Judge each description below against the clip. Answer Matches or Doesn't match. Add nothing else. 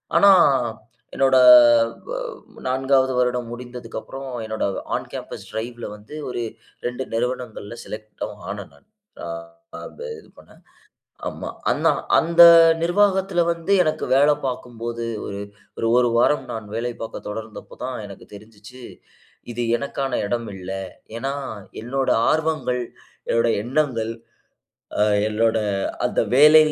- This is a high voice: Doesn't match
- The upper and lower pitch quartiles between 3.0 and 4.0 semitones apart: Matches